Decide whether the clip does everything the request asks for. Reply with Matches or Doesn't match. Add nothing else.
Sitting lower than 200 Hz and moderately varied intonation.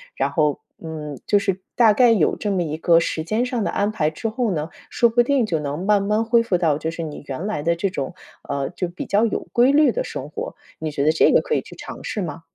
Doesn't match